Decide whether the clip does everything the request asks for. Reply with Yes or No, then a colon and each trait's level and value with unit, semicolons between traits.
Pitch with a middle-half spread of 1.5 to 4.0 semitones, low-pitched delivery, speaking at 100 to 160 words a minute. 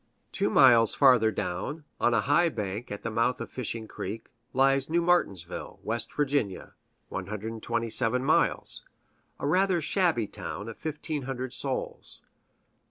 No: average, 4.6 semitones; low, 125 Hz; slow, 135 wpm